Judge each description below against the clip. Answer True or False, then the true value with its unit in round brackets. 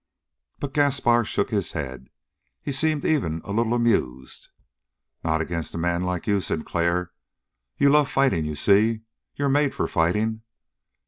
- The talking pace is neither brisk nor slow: True (145 wpm)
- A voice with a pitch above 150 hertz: False (105 Hz)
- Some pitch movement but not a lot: False (8.2 semitones)